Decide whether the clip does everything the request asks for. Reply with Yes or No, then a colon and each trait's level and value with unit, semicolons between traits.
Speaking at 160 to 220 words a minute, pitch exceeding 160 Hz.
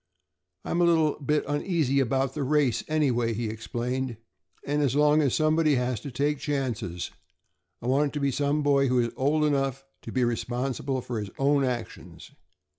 No: average, 180 wpm; low, 135 Hz